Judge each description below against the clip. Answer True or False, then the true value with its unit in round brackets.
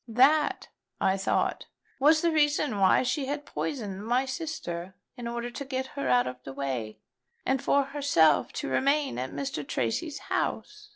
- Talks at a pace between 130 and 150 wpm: False (165 wpm)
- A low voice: False (245 Hz)